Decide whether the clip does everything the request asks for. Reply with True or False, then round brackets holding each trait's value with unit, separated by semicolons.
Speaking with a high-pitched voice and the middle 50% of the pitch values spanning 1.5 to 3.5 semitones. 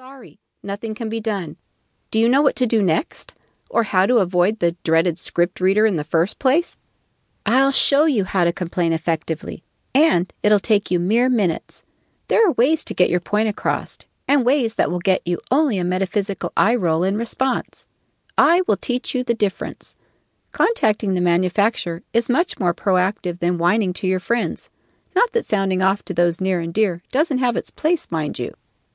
False (200 Hz; 5.2 semitones)